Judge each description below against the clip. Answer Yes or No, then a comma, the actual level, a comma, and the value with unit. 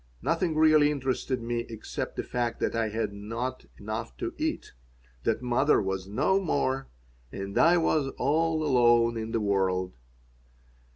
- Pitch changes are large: Yes, wide, 5.7 semitones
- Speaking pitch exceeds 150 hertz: No, low, 120 Hz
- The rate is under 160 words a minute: Yes, average, 150 wpm